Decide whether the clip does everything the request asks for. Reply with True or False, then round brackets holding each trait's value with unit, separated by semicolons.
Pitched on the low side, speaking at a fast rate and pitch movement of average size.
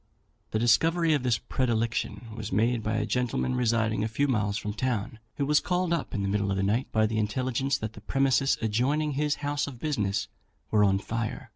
True (115 Hz; 210 wpm; 4.2 semitones)